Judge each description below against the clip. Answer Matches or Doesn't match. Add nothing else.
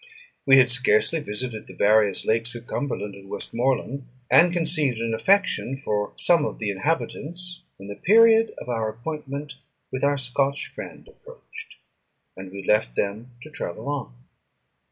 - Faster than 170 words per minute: Doesn't match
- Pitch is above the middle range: Doesn't match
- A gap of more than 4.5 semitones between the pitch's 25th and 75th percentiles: Matches